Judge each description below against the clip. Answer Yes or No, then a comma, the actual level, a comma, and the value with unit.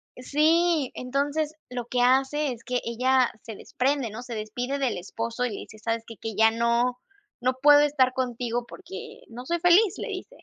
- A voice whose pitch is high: Yes, very high, 250 Hz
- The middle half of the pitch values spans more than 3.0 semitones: Yes, average, 3.5 semitones